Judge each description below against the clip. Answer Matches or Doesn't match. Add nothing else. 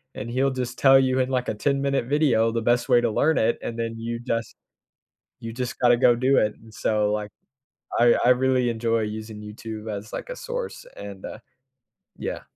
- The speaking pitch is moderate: Doesn't match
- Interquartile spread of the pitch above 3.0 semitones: Doesn't match